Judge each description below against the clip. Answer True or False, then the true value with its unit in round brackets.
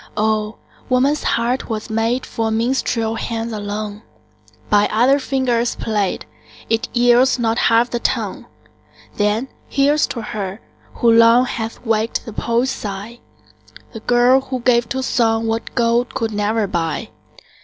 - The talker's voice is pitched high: True (230 Hz)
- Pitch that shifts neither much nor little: False (2.0 semitones)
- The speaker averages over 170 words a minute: False (140 wpm)